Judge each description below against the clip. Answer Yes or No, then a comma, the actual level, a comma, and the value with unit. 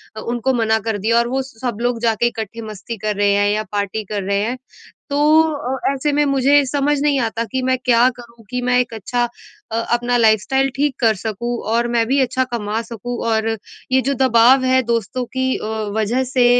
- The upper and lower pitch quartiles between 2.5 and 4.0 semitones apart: Yes, average, 2.8 semitones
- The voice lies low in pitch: No, high, 240 Hz